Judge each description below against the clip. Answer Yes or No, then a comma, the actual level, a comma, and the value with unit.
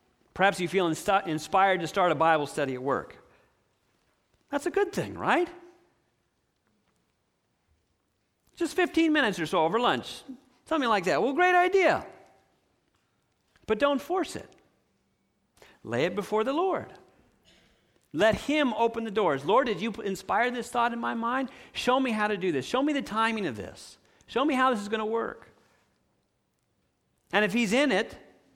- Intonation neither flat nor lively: No, wide, 6.5 semitones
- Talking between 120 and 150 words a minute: No, average, 160 wpm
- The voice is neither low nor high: No, high, 230 Hz